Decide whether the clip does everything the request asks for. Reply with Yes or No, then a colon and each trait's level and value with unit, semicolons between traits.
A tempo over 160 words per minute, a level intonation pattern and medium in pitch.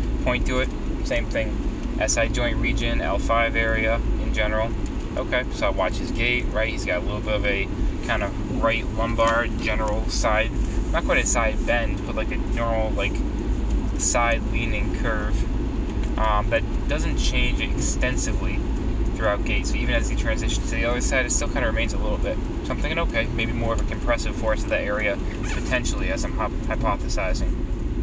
No: average, 185 wpm; narrow, 1.6 semitones; low, 110 Hz